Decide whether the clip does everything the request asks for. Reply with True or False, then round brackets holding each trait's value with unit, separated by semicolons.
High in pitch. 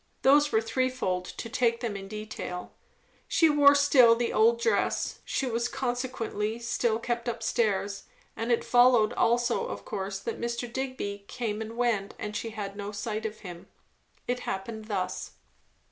True (230 Hz)